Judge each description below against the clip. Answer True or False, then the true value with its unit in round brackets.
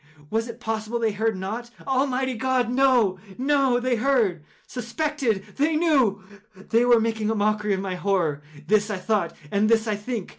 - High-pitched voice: True (225 Hz)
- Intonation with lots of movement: False (3.7 semitones)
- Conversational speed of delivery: True (150 wpm)